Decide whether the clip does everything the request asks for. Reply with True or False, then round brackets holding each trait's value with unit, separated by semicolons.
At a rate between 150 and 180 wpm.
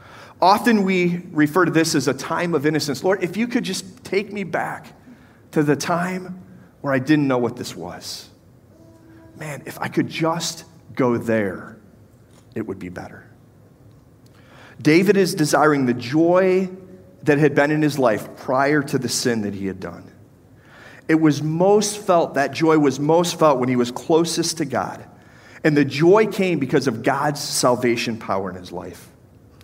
True (170 wpm)